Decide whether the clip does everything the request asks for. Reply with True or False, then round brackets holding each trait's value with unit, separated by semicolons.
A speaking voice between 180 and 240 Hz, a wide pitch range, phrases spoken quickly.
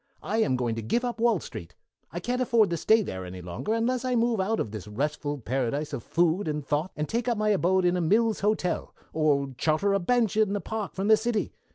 True (185 Hz; 7.2 semitones; 235 wpm)